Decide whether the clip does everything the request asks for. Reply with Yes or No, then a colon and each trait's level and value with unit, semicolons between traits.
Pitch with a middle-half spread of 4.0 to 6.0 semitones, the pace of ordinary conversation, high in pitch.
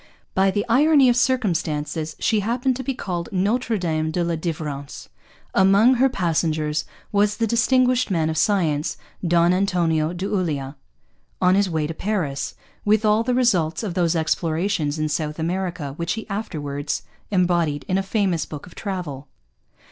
No: average, 5.0 semitones; average, 160 wpm; medium, 180 Hz